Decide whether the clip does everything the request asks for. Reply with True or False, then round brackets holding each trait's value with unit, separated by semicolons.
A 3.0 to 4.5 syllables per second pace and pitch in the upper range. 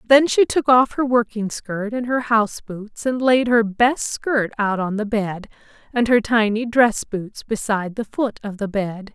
True (4.3 syllables/s; 225 Hz)